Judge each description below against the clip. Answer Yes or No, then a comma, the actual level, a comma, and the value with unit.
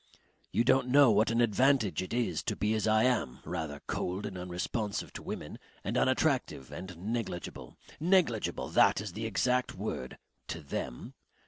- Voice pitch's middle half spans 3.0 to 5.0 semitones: No, wide, 5.6 semitones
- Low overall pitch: Yes, low, 110 Hz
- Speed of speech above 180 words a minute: No, average, 160 wpm